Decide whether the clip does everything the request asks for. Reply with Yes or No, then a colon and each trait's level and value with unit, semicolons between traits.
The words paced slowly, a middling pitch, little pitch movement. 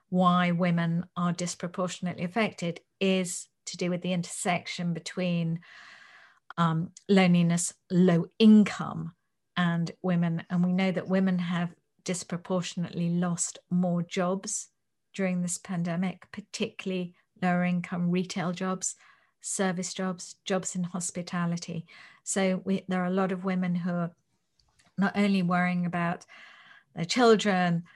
Yes: slow, 120 wpm; medium, 180 Hz; narrow, 1.3 semitones